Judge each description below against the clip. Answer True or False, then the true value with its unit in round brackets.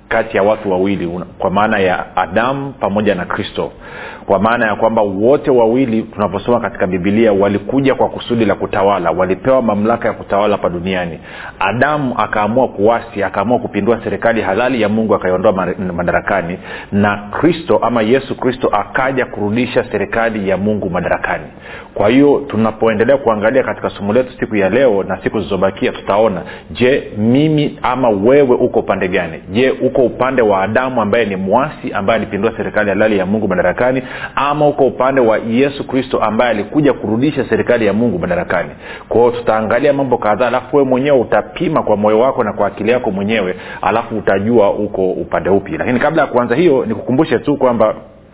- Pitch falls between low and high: False (110 Hz)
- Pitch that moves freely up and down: False (3.9 semitones)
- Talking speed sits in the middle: False (160 wpm)